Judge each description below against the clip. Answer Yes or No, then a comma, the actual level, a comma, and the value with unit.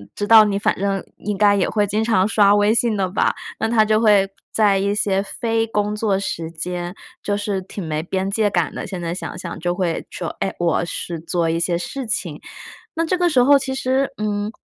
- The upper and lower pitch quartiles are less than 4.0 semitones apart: Yes, average, 3.3 semitones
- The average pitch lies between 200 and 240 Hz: Yes, high, 205 Hz